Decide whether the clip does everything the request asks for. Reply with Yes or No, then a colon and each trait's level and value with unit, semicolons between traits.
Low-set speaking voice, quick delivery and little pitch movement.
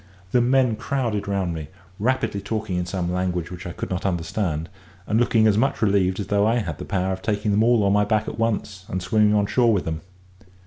No: low, 100 Hz; fast, 230 wpm; average, 3.3 semitones